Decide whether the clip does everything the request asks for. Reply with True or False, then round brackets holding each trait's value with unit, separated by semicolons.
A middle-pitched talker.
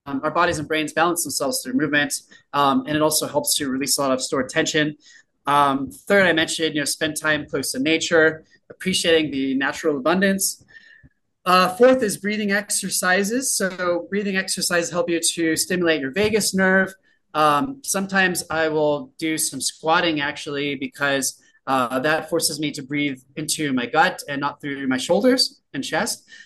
True (160 Hz)